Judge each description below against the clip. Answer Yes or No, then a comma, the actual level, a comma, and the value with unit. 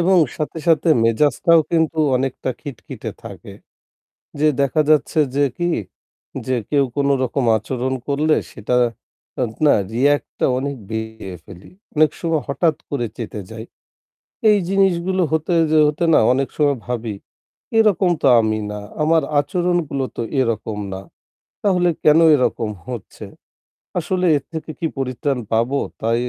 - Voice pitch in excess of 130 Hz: Yes, medium, 140 Hz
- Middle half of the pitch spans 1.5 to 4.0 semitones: No, average, 5.0 semitones